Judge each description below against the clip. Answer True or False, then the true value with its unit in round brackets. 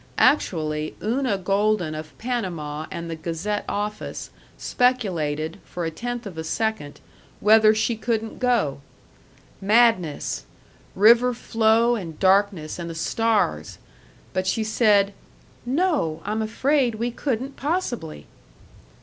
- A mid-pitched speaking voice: False (210 Hz)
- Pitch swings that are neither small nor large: False (6.0 semitones)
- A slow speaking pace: True (115 wpm)